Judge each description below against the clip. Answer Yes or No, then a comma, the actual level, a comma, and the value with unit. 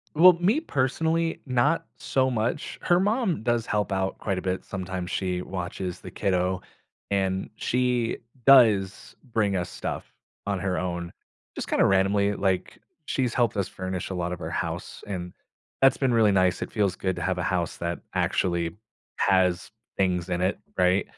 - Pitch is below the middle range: Yes, very low, 95 Hz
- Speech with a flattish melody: No, average, 5.1 semitones